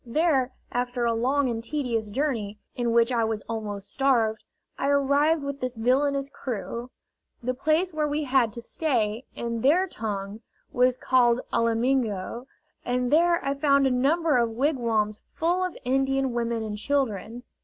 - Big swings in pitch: No, average, 3.5 semitones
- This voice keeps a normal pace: Yes, average, 155 wpm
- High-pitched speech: Yes, very high, 250 Hz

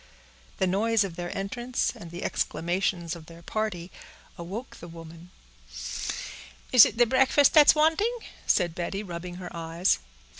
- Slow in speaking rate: No, average, 145 wpm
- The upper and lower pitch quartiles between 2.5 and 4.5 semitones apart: No, average, 5.1 semitones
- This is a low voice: No, medium, 185 Hz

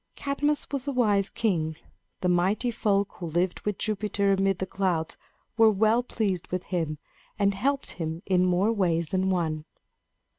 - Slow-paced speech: No, average, 160 wpm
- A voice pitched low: No, high, 195 Hz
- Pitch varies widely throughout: No, average, 3.5 semitones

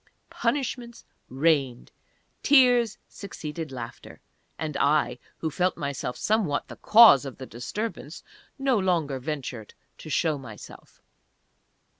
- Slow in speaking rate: Yes, slow, 110 wpm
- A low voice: No, medium, 155 Hz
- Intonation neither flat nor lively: No, wide, 8.3 semitones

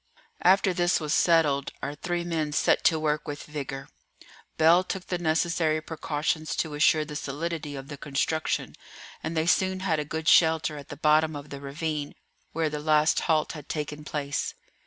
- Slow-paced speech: No, average, 180 wpm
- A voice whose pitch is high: No, medium, 155 Hz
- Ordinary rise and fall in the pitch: No, narrow, 1.8 semitones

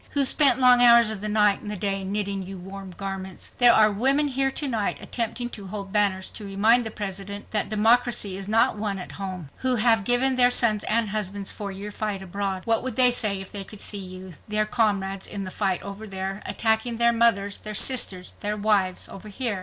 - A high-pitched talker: Yes, high, 210 Hz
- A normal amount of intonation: Yes, average, 3.0 semitones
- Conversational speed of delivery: No, fast, 215 wpm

